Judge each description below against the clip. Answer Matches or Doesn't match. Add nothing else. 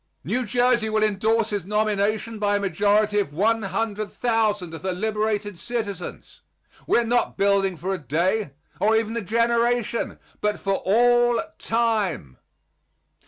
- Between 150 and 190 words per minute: Doesn't match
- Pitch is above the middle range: Matches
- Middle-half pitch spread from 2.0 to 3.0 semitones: Matches